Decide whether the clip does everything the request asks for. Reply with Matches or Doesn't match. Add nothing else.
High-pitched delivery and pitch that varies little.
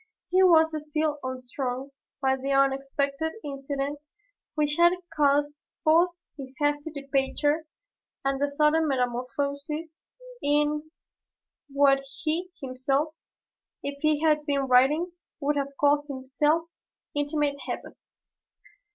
Matches